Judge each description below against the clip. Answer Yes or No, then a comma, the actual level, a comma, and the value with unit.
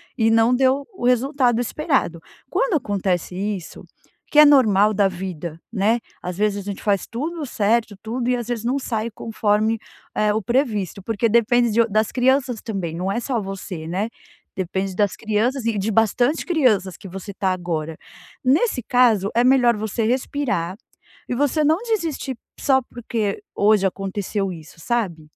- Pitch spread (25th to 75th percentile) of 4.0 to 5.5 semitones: Yes, average, 4.3 semitones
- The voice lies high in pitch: Yes, high, 220 Hz